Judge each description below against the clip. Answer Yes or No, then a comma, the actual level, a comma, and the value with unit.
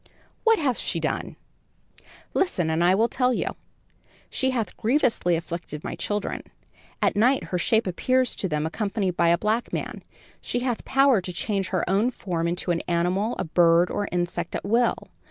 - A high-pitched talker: Yes, high, 195 Hz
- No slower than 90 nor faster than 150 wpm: No, average, 175 wpm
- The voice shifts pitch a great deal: Yes, wide, 5.7 semitones